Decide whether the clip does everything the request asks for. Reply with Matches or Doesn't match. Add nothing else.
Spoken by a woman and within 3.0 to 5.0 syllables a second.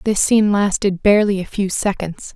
Doesn't match